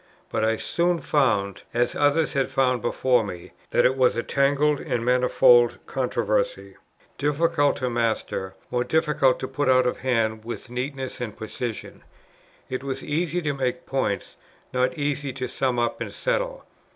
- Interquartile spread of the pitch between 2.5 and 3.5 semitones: Yes, average, 3.2 semitones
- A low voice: Yes, low, 130 Hz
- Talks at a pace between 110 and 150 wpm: No, average, 160 wpm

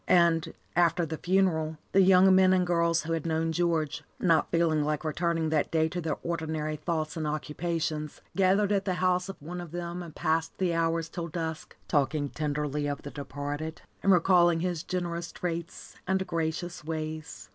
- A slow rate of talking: No, average, 180 wpm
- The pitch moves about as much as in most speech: No, narrow, 2.0 semitones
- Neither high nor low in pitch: Yes, medium, 165 Hz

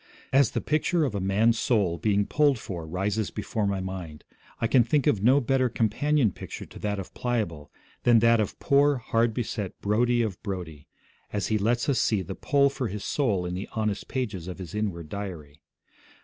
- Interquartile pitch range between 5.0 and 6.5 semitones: No, average, 4.3 semitones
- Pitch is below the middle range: Yes, low, 105 Hz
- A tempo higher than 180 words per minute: Yes, average, 195 wpm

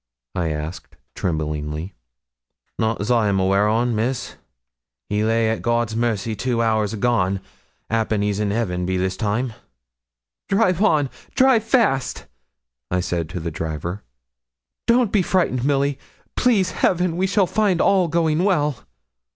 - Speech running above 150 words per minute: No, average, 140 wpm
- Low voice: Yes, low, 115 Hz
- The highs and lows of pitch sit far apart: Yes, wide, 9.0 semitones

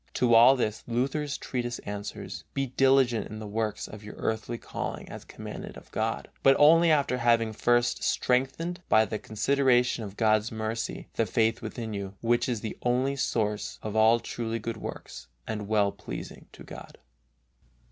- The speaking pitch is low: Yes, low, 115 Hz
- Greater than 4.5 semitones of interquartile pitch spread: No, narrow, 2.6 semitones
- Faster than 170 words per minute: No, average, 165 wpm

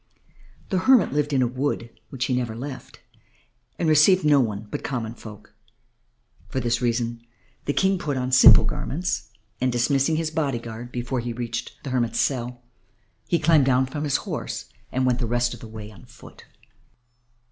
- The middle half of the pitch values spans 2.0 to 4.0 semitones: Yes, average, 3.6 semitones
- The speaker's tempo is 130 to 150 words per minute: No, average, 180 wpm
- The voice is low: Yes, low, 125 Hz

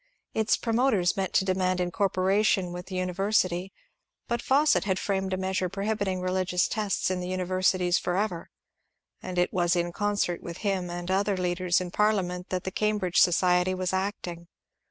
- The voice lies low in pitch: No, medium, 185 Hz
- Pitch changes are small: Yes, narrow, 1.8 semitones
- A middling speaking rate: Yes, average, 165 wpm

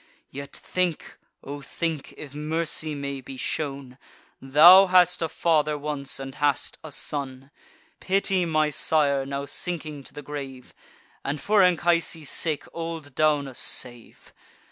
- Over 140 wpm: No, slow, 135 wpm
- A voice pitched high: No, medium, 150 Hz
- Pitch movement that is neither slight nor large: Yes, average, 3.0 semitones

